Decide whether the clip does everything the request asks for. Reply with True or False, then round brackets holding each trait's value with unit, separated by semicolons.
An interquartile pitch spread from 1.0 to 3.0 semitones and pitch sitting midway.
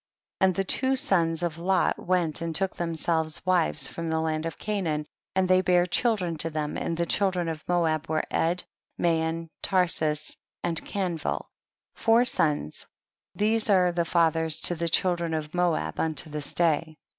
True (2.4 semitones; 170 Hz)